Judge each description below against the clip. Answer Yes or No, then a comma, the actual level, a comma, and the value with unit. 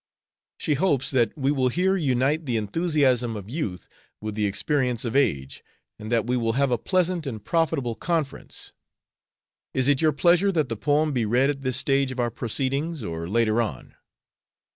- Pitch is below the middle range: Yes, low, 130 Hz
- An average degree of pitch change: Yes, average, 4.8 semitones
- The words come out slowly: No, average, 180 wpm